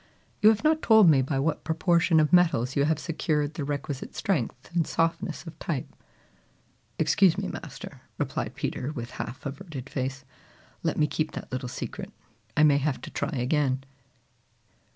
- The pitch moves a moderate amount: Yes, average, 3.6 semitones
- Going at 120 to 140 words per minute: No, average, 165 wpm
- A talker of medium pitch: Yes, medium, 150 Hz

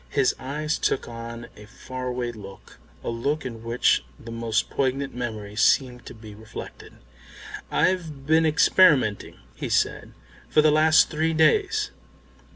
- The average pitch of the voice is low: Yes, low, 130 Hz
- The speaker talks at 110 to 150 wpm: Yes, average, 140 wpm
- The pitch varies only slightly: No, average, 4.9 semitones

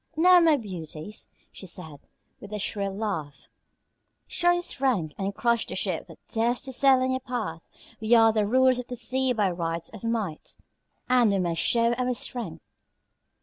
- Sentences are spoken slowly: No, average, 180 wpm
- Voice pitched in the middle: No, high, 225 Hz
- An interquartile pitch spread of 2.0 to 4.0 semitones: No, average, 5.1 semitones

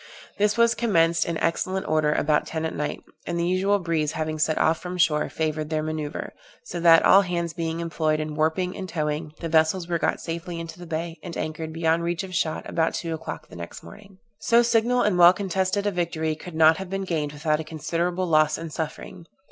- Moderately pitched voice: Yes, medium, 165 Hz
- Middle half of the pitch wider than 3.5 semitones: No, narrow, 2.4 semitones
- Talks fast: Yes, fast, 215 wpm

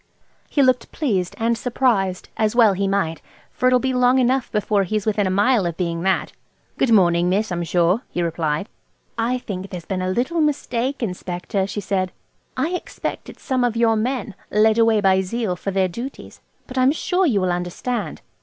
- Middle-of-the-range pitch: No, high, 210 Hz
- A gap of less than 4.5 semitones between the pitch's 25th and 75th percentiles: No, average, 5.1 semitones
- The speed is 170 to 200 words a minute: Yes, average, 185 wpm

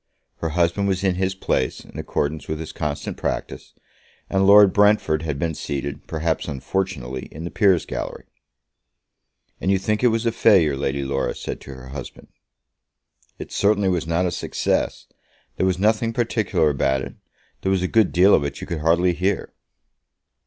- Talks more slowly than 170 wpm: No, average, 175 wpm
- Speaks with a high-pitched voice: No, very low, 85 Hz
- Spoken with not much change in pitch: No, average, 4.6 semitones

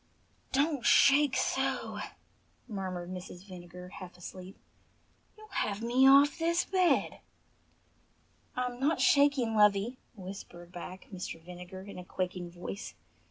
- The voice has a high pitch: Yes, high, 200 Hz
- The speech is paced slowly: Yes, slow, 115 wpm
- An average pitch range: No, wide, 6.8 semitones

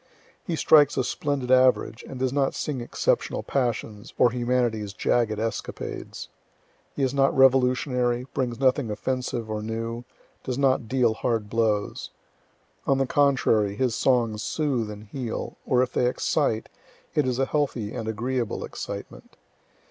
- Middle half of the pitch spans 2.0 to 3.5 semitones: Yes, average, 2.8 semitones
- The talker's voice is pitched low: Yes, low, 125 Hz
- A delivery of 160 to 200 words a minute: No, average, 145 wpm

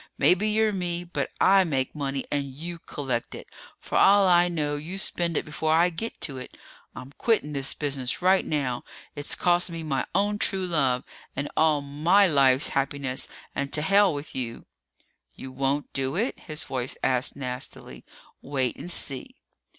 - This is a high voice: No, medium, 150 Hz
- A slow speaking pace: No, average, 175 wpm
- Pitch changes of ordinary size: Yes, average, 4.6 semitones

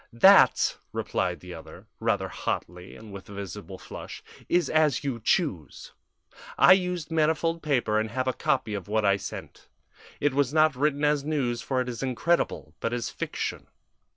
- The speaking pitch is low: Yes, low, 130 Hz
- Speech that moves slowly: No, average, 170 wpm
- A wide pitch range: Yes, wide, 6.2 semitones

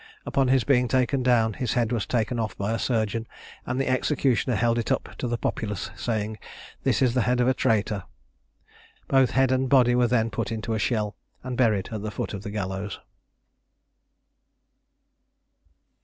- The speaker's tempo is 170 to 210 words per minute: Yes, average, 180 wpm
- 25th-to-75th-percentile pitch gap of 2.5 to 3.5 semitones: Yes, average, 2.8 semitones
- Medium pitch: No, low, 115 Hz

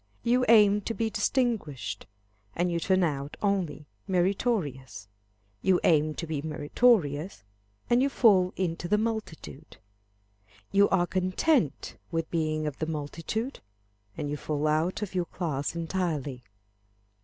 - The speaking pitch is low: No, medium, 175 Hz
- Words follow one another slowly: Yes, slow, 130 wpm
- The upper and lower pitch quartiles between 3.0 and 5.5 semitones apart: Yes, average, 5.1 semitones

